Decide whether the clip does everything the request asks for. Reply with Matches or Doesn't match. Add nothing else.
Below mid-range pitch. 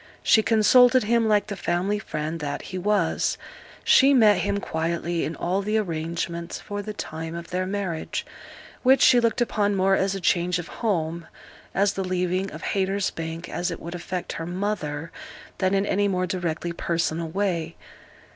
Doesn't match